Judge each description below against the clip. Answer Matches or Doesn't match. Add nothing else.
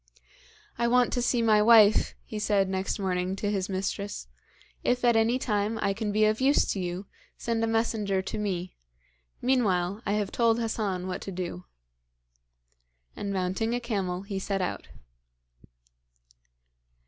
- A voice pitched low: Doesn't match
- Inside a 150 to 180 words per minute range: Matches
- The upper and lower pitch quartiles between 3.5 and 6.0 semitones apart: Doesn't match